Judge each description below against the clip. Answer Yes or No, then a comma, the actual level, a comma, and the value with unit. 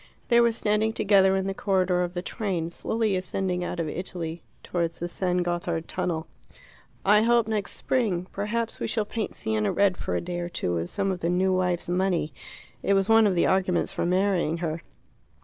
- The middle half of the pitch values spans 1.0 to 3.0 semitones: Yes, average, 2.7 semitones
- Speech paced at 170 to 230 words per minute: Yes, average, 200 wpm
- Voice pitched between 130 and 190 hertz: Yes, medium, 185 Hz